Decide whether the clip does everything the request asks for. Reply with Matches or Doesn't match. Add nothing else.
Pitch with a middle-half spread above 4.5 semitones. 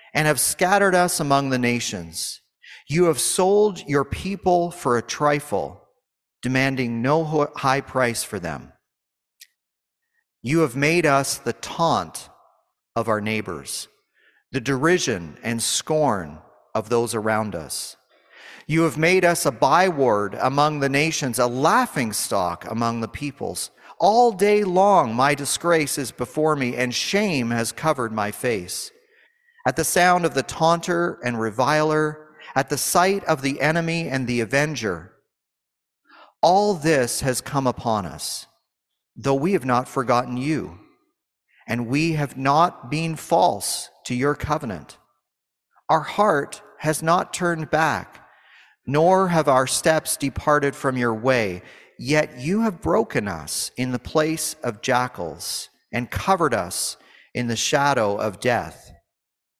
Matches